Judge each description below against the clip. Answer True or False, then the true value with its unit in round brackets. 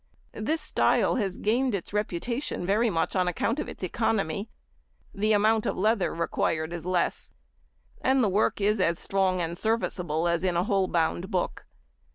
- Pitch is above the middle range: True (195 Hz)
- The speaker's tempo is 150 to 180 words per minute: True (170 wpm)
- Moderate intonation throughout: True (4.0 semitones)